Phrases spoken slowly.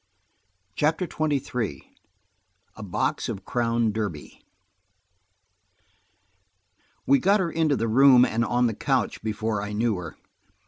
Yes: slow, 120 wpm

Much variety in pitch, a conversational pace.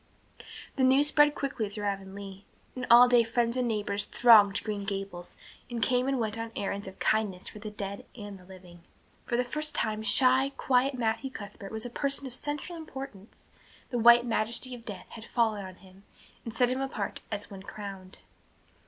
No: average, 3.9 semitones; average, 185 wpm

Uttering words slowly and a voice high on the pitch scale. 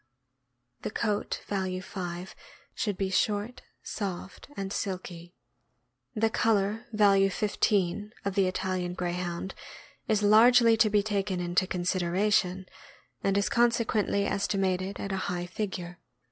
Yes: slow, 125 wpm; high, 195 Hz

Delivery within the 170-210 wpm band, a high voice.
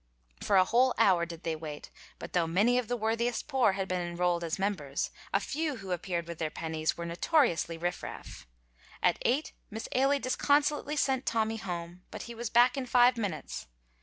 Yes: average, 195 wpm; high, 200 Hz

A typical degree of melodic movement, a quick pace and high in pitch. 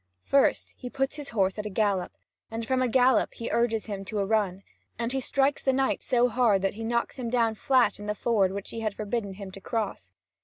Yes: average, 3.7 semitones; fast, 235 wpm; high, 225 Hz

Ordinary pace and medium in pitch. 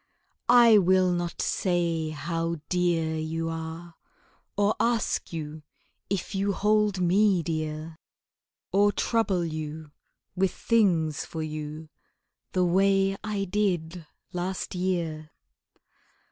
No: slow, 105 wpm; medium, 175 Hz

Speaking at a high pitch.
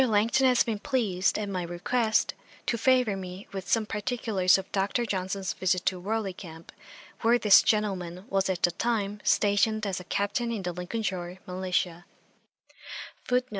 Yes: high, 200 Hz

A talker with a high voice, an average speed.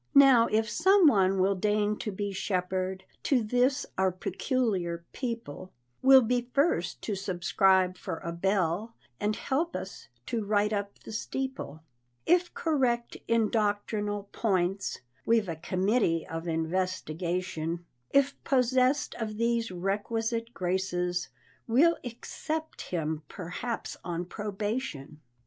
No: high, 205 Hz; slow, 125 wpm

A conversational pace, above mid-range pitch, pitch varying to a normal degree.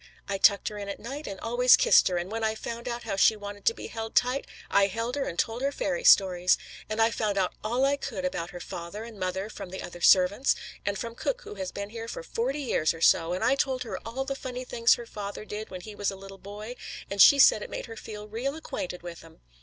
No: fast, 265 wpm; high, 215 Hz; average, 3.9 semitones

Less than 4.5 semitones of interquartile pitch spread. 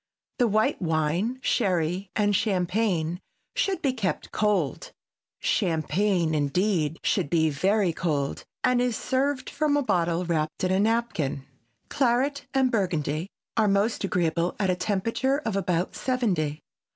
No: wide, 5.6 semitones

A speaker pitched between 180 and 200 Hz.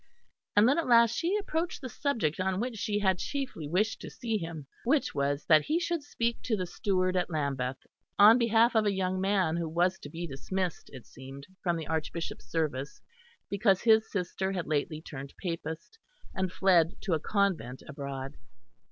Yes: medium, 185 Hz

